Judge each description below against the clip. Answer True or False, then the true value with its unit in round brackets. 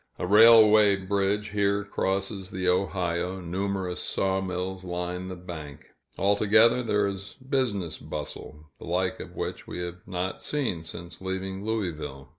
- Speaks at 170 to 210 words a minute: False (135 wpm)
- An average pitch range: False (2.3 semitones)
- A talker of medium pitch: False (95 Hz)